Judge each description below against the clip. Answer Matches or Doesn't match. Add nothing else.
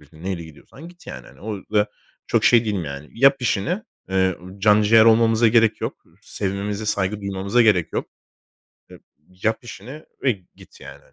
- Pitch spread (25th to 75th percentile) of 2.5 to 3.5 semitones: Matches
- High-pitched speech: Doesn't match